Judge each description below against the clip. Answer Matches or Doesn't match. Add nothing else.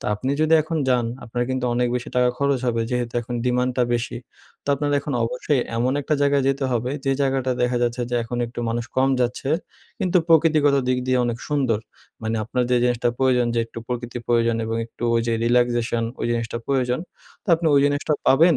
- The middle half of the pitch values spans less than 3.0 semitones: Matches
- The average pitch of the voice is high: Doesn't match